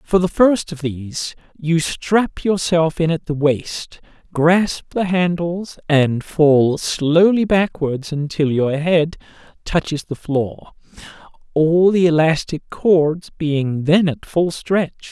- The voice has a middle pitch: Yes, medium, 165 Hz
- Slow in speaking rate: Yes, slow, 130 wpm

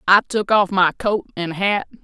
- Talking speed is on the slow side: No, fast, 205 wpm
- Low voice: No, high, 195 Hz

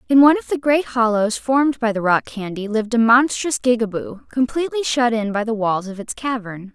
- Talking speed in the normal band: No, fast, 215 wpm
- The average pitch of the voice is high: Yes, high, 235 Hz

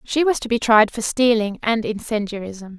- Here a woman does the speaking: Yes, female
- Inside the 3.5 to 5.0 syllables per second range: Yes, 4.9 syllables/s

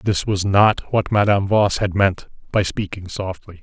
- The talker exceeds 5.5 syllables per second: No, 4.5 syllables/s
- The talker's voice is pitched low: Yes, low, 100 Hz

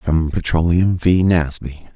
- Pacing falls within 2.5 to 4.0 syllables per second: Yes, 3.7 syllables/s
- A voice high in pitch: No, very low, 85 Hz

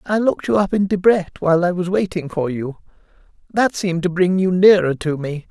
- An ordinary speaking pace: No, fast, 220 wpm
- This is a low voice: No, medium, 180 Hz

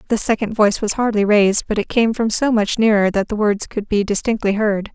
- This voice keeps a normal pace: No, fast, 240 wpm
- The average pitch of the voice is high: Yes, high, 210 Hz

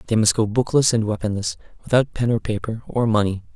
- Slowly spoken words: No, fast, 205 wpm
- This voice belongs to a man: Yes, male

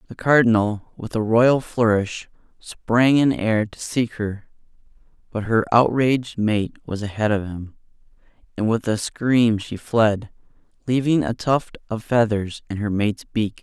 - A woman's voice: No, male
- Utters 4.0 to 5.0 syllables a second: Yes, 4.1 syllables/s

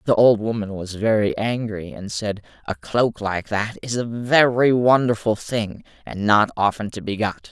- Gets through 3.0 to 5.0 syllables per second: Yes, 4.4 syllables/s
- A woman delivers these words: No, male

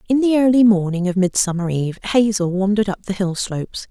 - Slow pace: No, average, 200 wpm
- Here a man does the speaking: No, female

